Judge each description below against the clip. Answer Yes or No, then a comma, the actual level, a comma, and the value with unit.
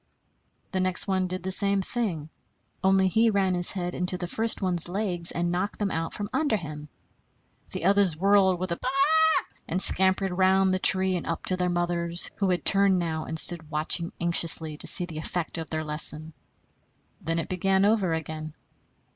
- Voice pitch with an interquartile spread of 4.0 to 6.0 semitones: No, narrow, 2.4 semitones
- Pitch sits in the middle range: Yes, medium, 180 Hz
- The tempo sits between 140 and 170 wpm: No, average, 195 wpm